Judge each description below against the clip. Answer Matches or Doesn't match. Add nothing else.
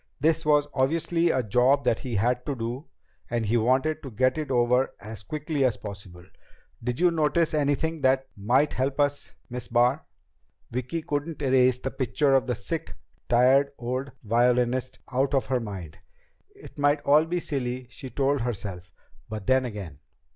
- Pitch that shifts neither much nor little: Matches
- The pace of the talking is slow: Doesn't match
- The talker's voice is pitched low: Matches